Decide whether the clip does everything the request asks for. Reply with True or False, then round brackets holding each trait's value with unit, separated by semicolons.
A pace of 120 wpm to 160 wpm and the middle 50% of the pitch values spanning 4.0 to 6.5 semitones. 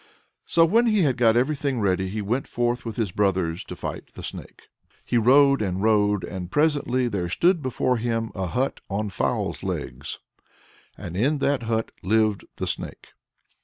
False (170 wpm; 5.2 semitones)